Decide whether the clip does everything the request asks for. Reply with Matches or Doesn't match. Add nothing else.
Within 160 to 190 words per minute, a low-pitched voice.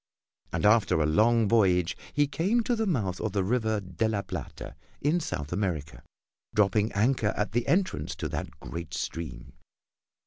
Matches